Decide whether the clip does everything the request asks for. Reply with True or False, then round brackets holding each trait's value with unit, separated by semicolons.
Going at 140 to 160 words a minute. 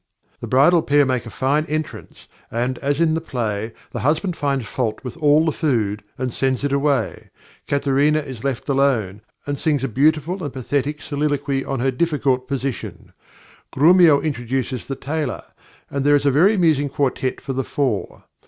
False (170 wpm)